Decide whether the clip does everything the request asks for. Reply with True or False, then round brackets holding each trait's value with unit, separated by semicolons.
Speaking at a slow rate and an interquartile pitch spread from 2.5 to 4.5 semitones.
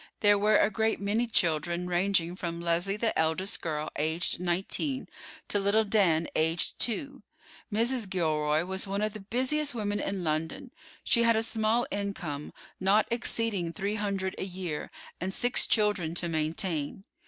False (155 wpm; 4.2 semitones)